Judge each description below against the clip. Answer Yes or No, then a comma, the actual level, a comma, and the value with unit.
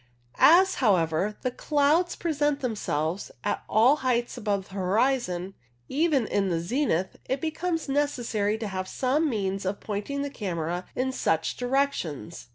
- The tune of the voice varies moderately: No, wide, 6.9 semitones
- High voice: Yes, high, 230 Hz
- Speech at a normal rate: Yes, average, 150 wpm